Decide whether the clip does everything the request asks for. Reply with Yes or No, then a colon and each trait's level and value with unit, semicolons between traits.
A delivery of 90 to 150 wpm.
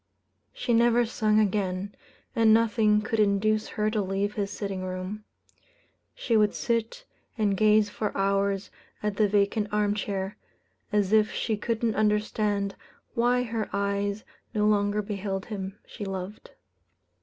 Yes: average, 140 wpm